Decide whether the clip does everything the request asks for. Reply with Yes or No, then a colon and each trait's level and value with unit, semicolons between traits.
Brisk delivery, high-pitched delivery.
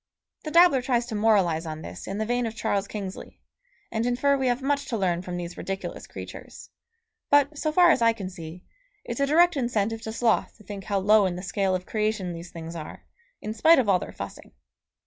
Yes: fast, 220 wpm; high, 215 Hz